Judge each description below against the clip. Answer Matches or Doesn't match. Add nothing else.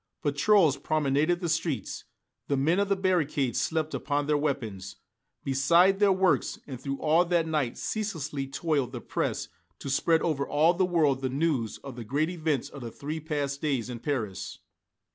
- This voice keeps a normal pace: Matches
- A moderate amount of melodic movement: Matches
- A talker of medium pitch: Matches